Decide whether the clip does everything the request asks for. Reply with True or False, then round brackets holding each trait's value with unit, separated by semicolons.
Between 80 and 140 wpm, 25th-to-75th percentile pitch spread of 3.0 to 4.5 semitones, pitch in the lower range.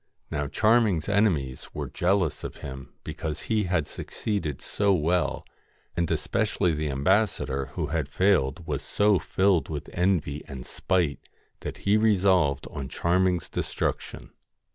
False (135 wpm; 5.3 semitones; 85 Hz)